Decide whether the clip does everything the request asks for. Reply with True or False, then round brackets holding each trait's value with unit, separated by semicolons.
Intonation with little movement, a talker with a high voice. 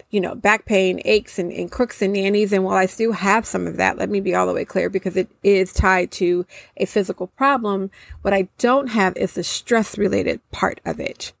True (2.2 semitones; 195 Hz)